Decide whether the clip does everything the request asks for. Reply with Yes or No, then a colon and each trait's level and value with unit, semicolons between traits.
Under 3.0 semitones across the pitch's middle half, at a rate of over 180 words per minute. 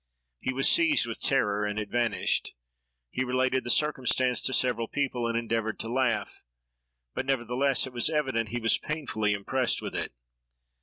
No: narrow, 2.5 semitones; average, 165 wpm